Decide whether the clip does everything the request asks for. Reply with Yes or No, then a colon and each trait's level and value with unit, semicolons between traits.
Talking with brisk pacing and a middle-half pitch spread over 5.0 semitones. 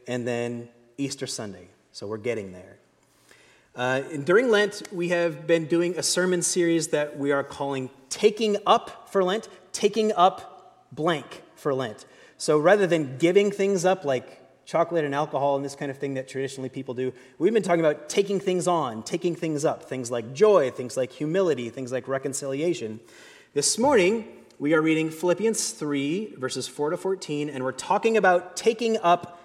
No: average, 175 wpm; wide, 5.5 semitones